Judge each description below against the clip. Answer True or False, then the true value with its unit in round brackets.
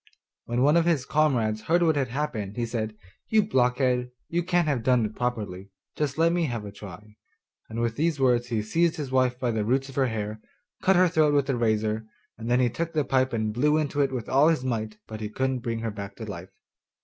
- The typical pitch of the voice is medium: False (125 Hz)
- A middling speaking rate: False (230 wpm)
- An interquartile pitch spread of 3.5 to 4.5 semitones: False (5.0 semitones)